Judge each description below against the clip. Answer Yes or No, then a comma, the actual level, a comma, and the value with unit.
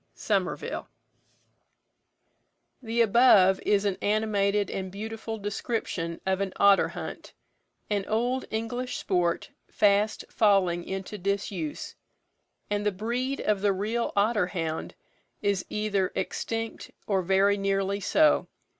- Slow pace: Yes, slow, 115 wpm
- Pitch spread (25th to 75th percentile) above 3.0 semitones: No, narrow, 2.4 semitones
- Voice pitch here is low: No, high, 200 Hz